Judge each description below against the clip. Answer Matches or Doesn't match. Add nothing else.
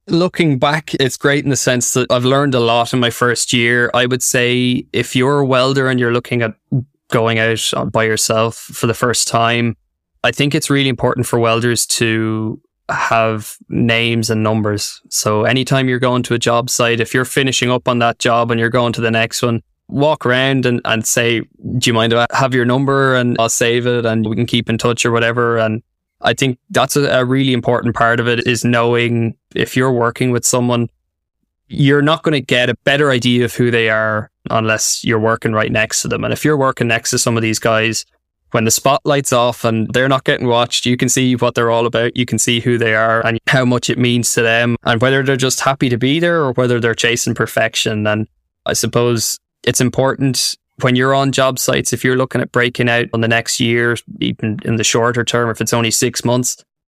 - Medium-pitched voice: Doesn't match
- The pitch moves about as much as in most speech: Doesn't match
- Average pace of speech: Doesn't match